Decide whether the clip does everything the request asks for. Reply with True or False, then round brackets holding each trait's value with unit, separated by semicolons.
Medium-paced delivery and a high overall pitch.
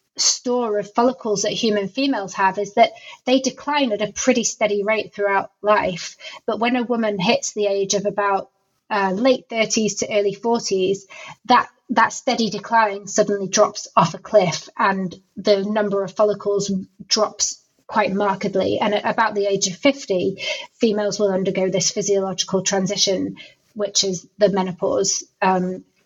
True (155 wpm; 205 Hz)